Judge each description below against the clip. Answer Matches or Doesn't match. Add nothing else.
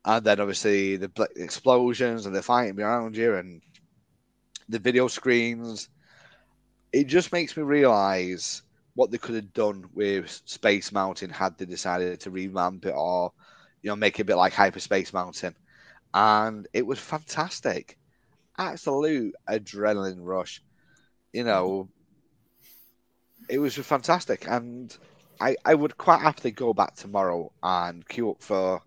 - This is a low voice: Matches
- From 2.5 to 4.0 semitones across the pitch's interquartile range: Doesn't match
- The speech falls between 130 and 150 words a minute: Matches